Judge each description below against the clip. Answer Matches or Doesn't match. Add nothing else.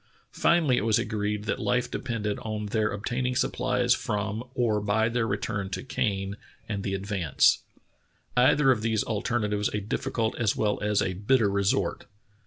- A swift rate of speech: Doesn't match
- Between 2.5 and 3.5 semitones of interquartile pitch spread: Matches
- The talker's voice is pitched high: Doesn't match